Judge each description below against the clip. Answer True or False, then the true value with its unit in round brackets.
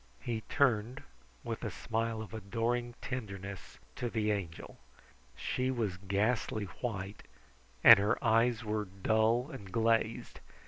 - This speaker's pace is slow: True (125 wpm)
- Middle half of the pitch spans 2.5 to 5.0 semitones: True (2.9 semitones)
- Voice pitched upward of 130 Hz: False (110 Hz)